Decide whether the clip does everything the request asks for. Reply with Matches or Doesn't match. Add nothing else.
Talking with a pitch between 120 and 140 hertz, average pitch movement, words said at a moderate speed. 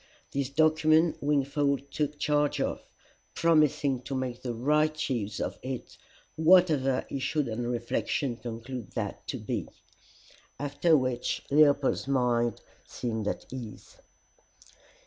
Doesn't match